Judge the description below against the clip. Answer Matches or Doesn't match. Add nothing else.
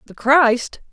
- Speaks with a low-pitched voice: Doesn't match